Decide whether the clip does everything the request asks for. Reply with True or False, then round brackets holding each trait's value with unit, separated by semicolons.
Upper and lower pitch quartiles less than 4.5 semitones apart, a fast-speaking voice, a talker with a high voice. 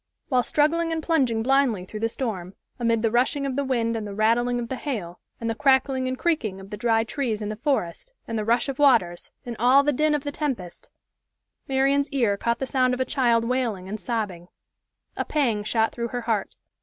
True (3.8 semitones; 220 wpm; 240 Hz)